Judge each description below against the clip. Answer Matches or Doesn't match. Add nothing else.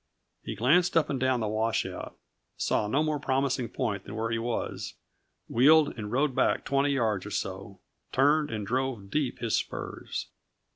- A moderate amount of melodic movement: Matches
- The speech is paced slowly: Doesn't match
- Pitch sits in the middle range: Doesn't match